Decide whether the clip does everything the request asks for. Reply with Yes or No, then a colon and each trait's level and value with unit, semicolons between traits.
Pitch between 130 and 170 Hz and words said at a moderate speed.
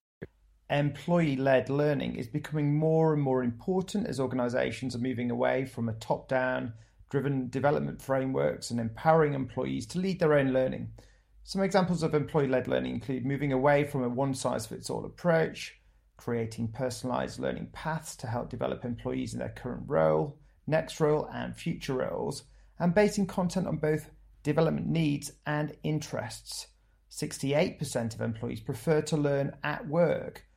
Yes: medium, 140 Hz; average, 145 wpm